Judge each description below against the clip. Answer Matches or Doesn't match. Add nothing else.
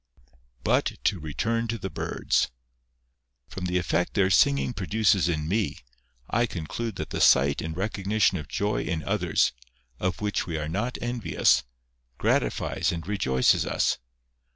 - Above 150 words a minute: Doesn't match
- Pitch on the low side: Matches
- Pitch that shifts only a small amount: Doesn't match